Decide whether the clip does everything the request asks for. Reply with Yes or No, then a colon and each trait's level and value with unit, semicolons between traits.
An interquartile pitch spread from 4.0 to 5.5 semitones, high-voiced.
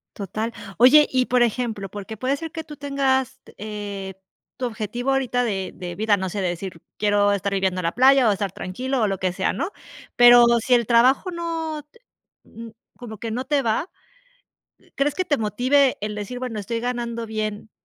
Yes: average, 4.3 semitones; high, 230 Hz